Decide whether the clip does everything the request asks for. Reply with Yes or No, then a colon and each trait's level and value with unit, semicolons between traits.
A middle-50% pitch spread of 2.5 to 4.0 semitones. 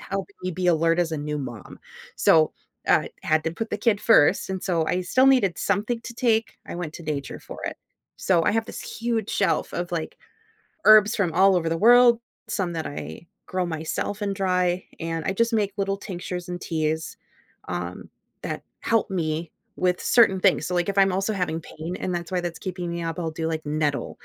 Yes: average, 3.5 semitones